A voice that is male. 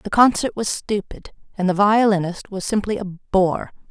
No: female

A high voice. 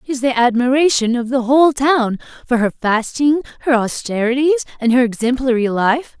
Yes: very high, 250 Hz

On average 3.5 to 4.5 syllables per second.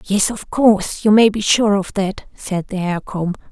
Yes: 4.4 syllables/s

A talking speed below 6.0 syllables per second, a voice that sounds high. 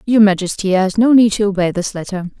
No: 6.1 syllables/s; high, 200 Hz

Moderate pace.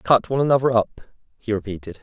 Yes: average, 180 wpm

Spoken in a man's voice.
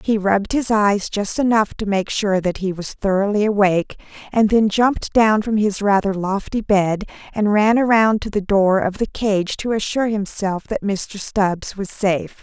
No: female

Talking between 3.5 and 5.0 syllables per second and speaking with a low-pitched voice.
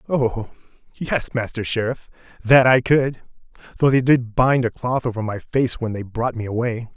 Yes: 4.6 syllables/s; low, 120 Hz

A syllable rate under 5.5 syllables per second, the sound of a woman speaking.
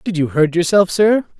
No: 5.0 syllables/s; male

